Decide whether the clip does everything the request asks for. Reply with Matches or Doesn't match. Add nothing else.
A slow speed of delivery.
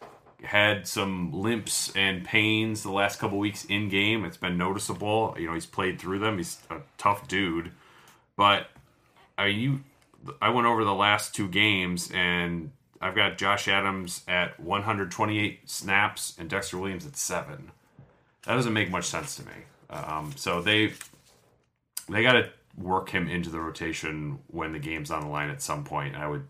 Doesn't match